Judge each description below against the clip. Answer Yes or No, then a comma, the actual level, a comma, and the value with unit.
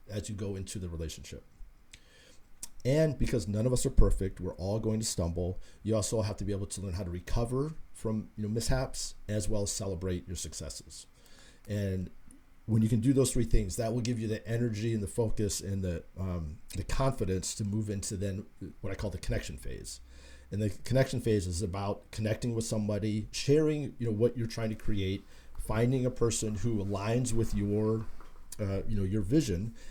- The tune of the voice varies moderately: Yes, average, 3.3 semitones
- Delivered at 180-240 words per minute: Yes, average, 200 wpm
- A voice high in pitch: No, low, 105 Hz